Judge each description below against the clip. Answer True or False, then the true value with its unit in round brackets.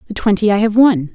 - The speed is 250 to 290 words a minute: True (260 wpm)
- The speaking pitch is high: True (210 Hz)